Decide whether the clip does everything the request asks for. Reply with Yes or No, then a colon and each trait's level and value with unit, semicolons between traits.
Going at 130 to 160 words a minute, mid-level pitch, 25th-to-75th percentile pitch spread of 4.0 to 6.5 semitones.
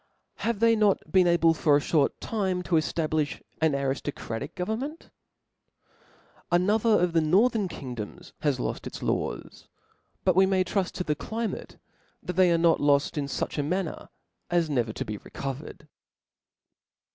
Yes: average, 155 wpm; medium, 170 Hz; average, 4.7 semitones